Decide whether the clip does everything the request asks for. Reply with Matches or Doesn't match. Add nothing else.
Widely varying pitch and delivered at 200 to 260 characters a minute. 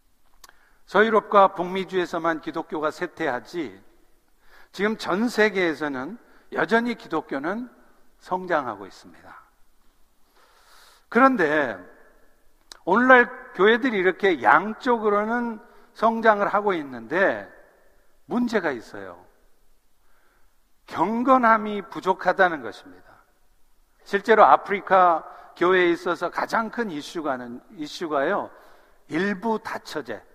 Doesn't match